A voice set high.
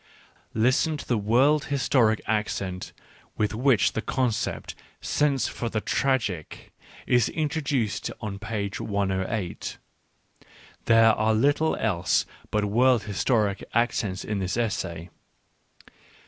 No: low, 110 Hz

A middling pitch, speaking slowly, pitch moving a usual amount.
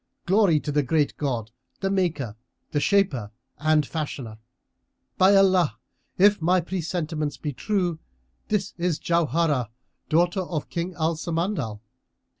Yes: medium, 165 Hz; slow, 125 wpm; average, 4.0 semitones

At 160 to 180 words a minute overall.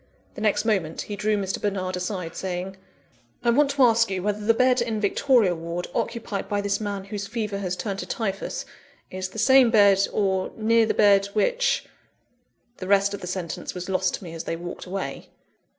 No: average, 200 wpm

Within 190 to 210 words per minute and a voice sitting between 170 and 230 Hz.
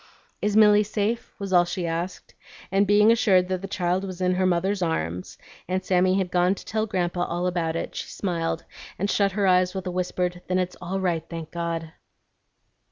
Yes: average, 200 wpm; medium, 185 Hz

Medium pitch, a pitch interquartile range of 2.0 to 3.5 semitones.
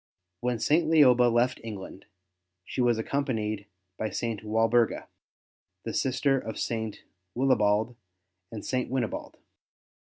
No: low, 120 Hz; average, 2.8 semitones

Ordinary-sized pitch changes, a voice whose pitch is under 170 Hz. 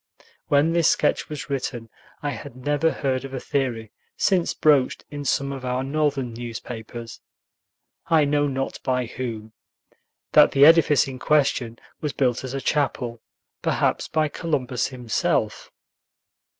Yes: average, 3.0 semitones; low, 135 Hz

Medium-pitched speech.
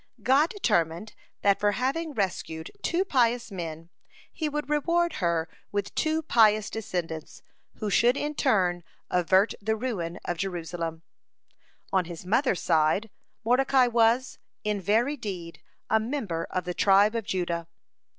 No: high, 210 Hz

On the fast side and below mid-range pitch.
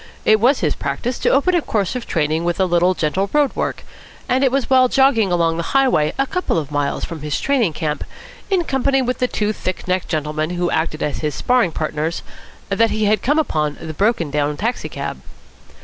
No: fast, 210 wpm; medium, 185 Hz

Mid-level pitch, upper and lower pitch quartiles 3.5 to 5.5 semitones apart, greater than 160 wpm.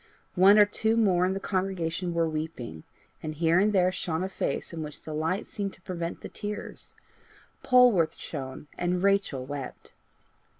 Yes: medium, 180 Hz; average, 3.8 semitones; average, 170 wpm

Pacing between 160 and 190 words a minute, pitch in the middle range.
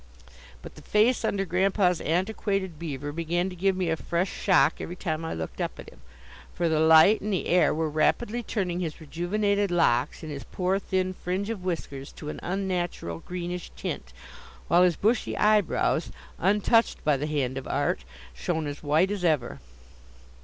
Yes: average, 175 wpm; medium, 175 Hz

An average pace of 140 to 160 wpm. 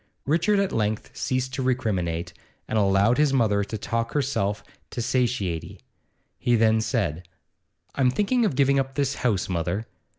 Yes: average, 155 wpm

